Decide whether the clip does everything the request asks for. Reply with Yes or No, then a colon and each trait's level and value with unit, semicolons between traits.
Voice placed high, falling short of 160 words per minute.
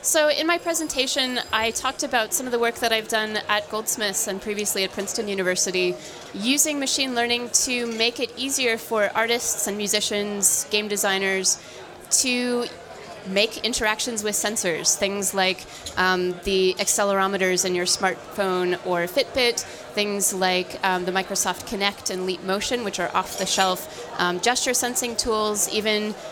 Yes: high, 210 Hz; average, 150 wpm